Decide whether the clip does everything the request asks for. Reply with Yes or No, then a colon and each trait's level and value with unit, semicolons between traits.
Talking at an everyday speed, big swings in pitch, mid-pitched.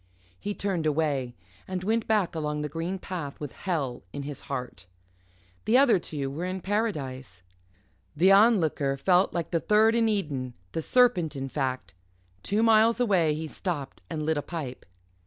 Yes: average, 165 wpm; wide, 6.0 semitones; medium, 165 Hz